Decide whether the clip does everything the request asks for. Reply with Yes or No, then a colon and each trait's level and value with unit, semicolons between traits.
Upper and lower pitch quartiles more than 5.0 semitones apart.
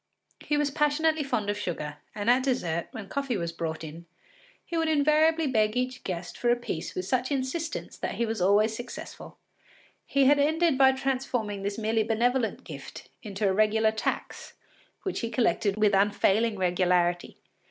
Yes: wide, 5.4 semitones